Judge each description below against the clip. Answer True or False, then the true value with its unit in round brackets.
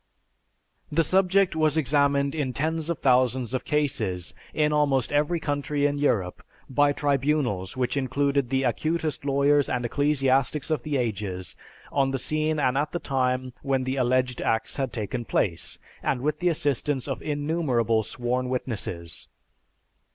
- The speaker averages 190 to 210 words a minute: False (150 wpm)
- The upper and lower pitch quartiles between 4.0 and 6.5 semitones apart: False (3.1 semitones)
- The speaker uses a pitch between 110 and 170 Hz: True (135 Hz)